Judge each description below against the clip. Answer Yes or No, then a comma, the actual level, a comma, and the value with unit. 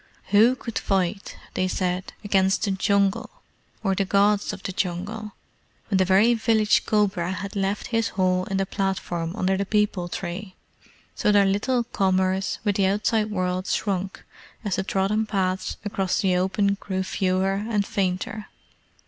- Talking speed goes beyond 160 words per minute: No, average, 155 wpm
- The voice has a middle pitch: No, high, 195 Hz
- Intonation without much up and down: Yes, narrow, 1.8 semitones